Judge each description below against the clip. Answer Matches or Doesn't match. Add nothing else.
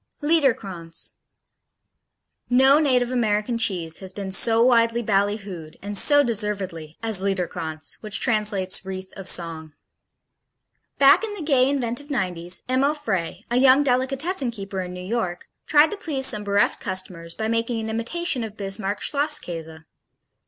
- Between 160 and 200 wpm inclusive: Doesn't match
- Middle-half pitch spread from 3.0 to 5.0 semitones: Doesn't match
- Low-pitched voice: Doesn't match